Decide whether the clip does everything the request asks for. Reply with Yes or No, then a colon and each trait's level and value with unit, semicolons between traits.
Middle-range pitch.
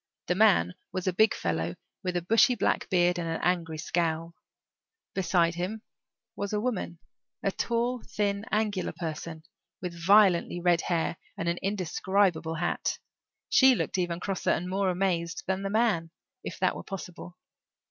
Yes: medium, 180 Hz